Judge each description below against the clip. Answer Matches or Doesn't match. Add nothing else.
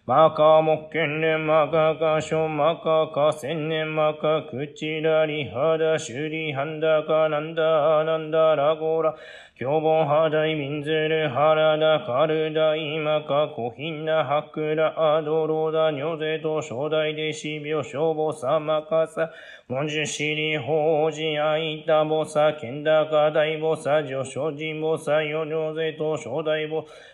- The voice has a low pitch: Doesn't match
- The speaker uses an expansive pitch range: Doesn't match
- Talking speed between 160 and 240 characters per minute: Doesn't match